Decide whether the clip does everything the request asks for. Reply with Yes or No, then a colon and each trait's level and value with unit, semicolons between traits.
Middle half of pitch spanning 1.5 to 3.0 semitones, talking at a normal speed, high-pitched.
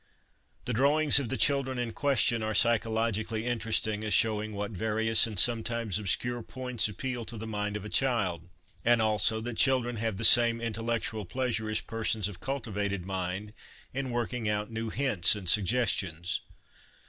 No: narrow, 2.4 semitones; average, 160 wpm; low, 110 Hz